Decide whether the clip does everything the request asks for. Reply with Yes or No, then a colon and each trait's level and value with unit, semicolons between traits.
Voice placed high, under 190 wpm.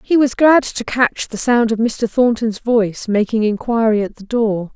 No: high, 225 Hz; average, 200 wpm